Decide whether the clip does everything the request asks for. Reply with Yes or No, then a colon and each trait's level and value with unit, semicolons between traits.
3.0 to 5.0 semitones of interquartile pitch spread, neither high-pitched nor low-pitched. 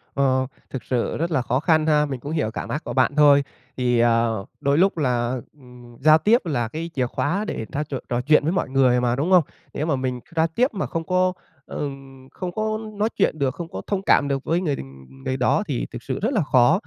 Yes: average, 4.7 semitones; medium, 145 Hz